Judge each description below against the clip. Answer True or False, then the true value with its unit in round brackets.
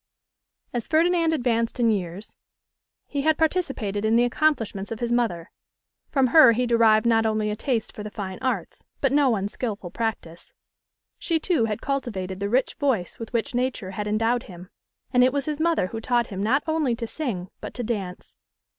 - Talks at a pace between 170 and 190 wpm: True (185 wpm)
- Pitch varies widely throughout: False (4.1 semitones)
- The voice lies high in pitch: True (230 Hz)